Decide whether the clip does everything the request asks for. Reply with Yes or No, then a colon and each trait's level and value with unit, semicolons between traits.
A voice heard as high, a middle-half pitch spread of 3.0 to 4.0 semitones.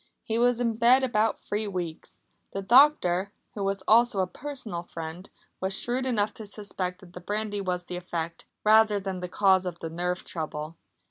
Yes: high, 195 Hz; average, 3.7 semitones